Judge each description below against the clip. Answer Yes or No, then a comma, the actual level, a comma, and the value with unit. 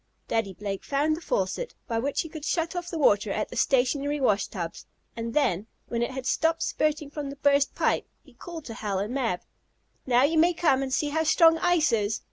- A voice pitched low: No, very high, 280 Hz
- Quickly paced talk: Yes, fast, 220 wpm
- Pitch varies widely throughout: Yes, wide, 5.7 semitones